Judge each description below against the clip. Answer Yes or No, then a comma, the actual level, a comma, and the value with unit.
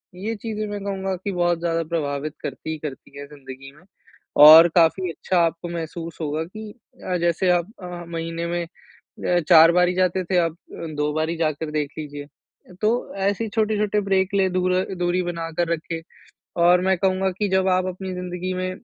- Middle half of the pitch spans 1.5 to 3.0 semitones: Yes, narrow, 2.5 semitones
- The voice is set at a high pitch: No, medium, 175 Hz